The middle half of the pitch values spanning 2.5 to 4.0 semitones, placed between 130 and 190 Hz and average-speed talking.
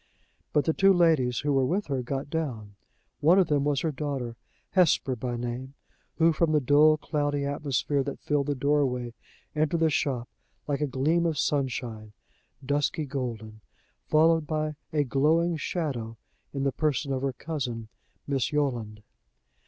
Yes: average, 3.3 semitones; medium, 140 Hz; average, 160 wpm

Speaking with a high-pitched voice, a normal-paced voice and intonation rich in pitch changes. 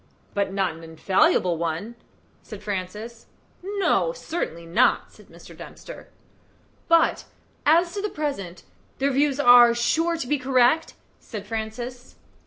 No: high, 240 Hz; slow, 130 wpm; wide, 7.7 semitones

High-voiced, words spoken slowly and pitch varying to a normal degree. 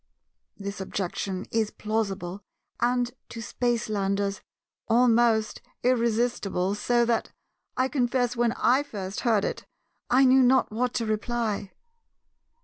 Yes: high, 230 Hz; slow, 115 wpm; average, 3.2 semitones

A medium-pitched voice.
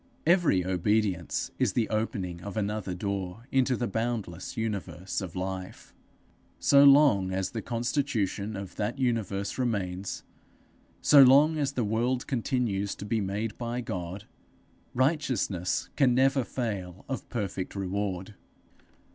No: low, 105 Hz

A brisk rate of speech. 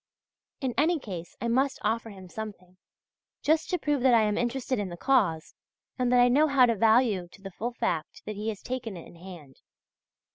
Yes: fast, 215 wpm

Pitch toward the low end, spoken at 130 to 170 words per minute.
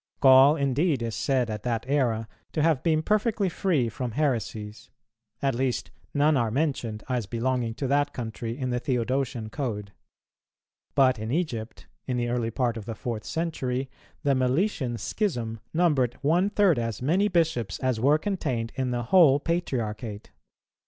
Yes: low, 130 Hz; average, 160 wpm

